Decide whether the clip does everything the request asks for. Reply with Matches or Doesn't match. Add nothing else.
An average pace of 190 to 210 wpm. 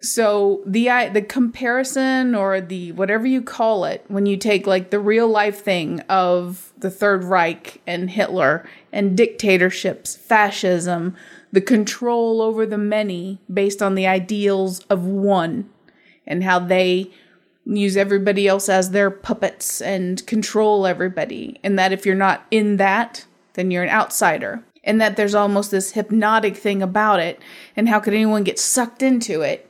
Doesn't match